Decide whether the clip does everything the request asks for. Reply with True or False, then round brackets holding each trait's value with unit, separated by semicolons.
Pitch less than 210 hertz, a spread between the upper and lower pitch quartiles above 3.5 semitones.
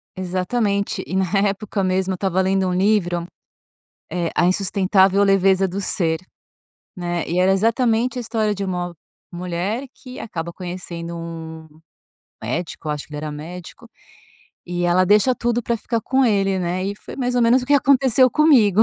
True (190 Hz; 4.1 semitones)